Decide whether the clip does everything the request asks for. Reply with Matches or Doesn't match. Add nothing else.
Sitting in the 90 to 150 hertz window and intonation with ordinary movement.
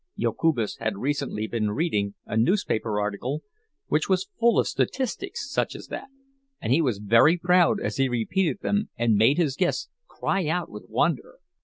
Doesn't match